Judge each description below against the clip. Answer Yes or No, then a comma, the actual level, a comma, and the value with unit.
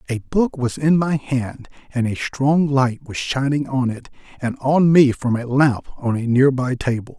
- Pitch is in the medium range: No, low, 130 Hz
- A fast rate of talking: Yes, fast, 210 wpm